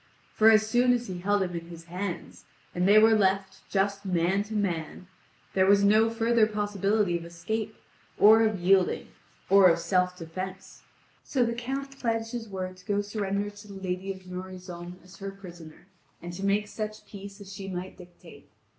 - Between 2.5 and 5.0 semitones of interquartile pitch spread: Yes, average, 2.8 semitones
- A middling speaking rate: Yes, average, 190 wpm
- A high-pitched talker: Yes, high, 195 Hz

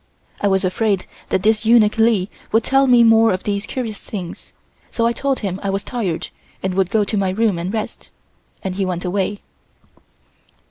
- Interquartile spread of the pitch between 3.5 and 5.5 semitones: No, average, 3.0 semitones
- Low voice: No, high, 205 Hz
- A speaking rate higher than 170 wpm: Yes, average, 190 wpm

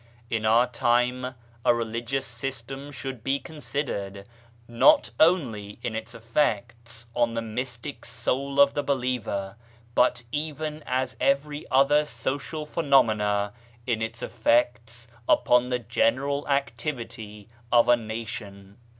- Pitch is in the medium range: No, low, 120 Hz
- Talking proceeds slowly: Yes, slow, 125 wpm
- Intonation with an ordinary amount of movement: Yes, average, 3.4 semitones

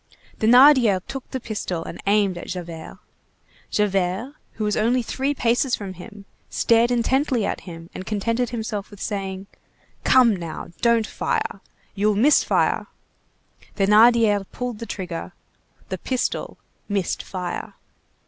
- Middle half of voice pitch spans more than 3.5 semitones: Yes, average, 4.0 semitones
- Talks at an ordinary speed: No, slow, 130 wpm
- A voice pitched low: No, high, 215 Hz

